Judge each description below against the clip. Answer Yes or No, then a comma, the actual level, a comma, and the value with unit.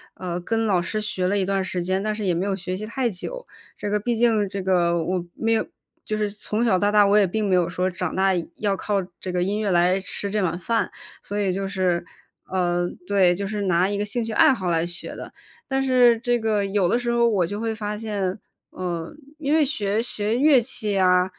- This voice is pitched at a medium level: No, high, 200 Hz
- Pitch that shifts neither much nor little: Yes, average, 3.2 semitones